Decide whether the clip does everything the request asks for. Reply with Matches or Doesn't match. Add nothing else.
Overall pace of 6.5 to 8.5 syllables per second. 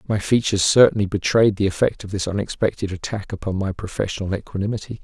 Matches